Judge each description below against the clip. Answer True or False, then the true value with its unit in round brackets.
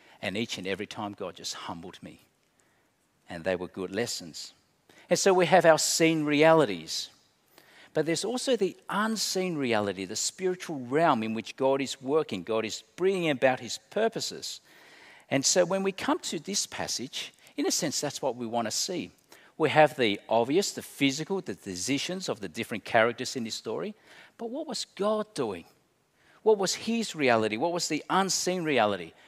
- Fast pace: False (180 wpm)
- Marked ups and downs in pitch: True (8.5 semitones)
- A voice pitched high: False (155 Hz)